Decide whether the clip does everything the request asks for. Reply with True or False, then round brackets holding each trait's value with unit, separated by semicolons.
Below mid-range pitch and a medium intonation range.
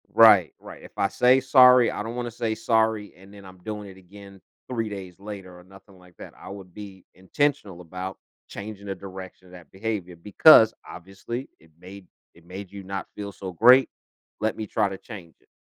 True (100 Hz; 3.0 semitones)